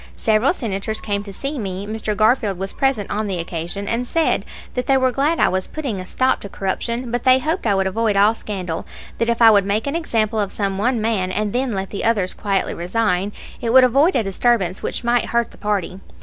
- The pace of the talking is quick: Yes, fast, 225 wpm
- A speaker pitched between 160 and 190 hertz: No, high, 215 Hz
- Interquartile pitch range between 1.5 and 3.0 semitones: No, average, 3.7 semitones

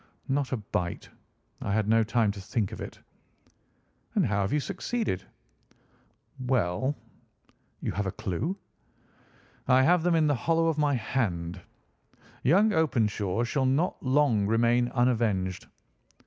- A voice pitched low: Yes, low, 120 Hz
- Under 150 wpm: Yes, slow, 135 wpm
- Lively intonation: Yes, wide, 6.2 semitones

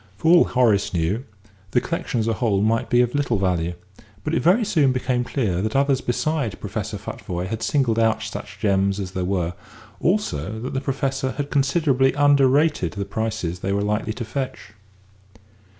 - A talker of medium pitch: No, low, 120 Hz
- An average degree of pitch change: No, wide, 5.7 semitones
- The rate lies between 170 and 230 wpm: Yes, average, 180 wpm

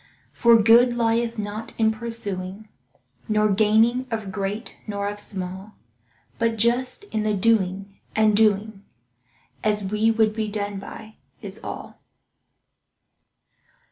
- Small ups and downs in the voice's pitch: Yes, narrow, 1.9 semitones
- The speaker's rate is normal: No, slow, 120 wpm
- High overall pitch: Yes, high, 215 Hz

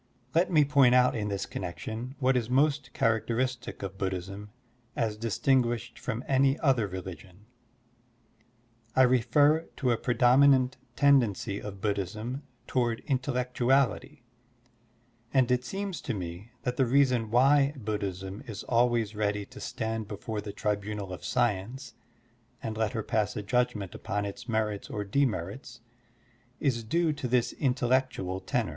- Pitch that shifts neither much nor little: Yes, average, 4.0 semitones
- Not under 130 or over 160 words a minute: Yes, average, 140 wpm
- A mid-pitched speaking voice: No, low, 120 Hz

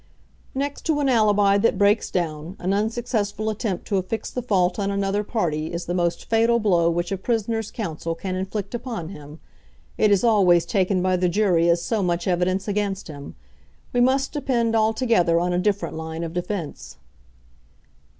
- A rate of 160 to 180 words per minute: Yes, average, 175 wpm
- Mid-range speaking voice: No, high, 195 Hz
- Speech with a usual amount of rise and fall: Yes, average, 4.1 semitones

